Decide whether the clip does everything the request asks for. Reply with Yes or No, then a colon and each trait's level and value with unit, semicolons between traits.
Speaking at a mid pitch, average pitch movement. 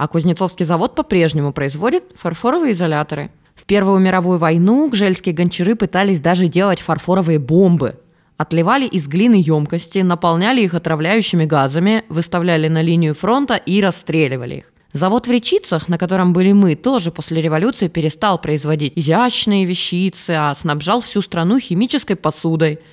Yes: medium, 175 Hz; average, 3.8 semitones